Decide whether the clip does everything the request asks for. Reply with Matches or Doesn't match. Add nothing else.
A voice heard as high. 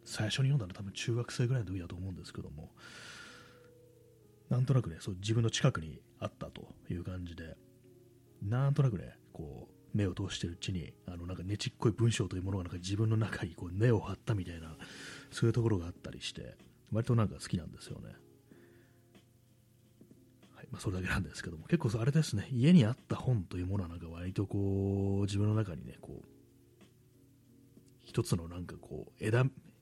Doesn't match